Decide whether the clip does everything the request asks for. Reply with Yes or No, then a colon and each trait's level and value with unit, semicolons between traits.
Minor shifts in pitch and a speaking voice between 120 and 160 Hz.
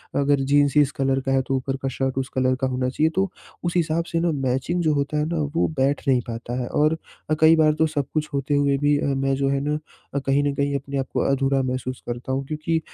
Yes: narrow, 2.3 semitones; medium, 140 Hz